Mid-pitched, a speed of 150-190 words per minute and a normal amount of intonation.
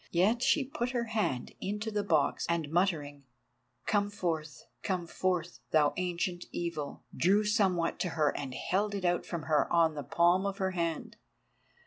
Yes: medium, 175 Hz; average, 160 wpm; average, 4.0 semitones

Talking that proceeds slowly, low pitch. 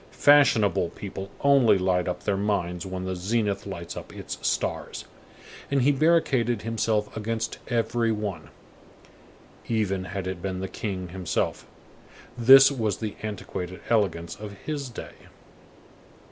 Yes: slow, 130 wpm; low, 105 Hz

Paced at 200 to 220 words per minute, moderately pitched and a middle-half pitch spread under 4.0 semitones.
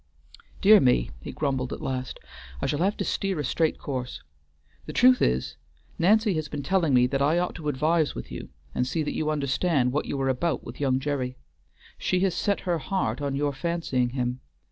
No: fast, 205 wpm; medium, 145 Hz; average, 4.7 semitones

